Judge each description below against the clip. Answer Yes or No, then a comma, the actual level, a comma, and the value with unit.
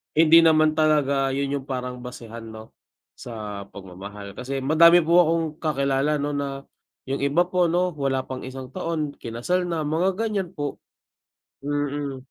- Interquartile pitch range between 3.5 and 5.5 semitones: Yes, average, 3.9 semitones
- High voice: No, medium, 145 Hz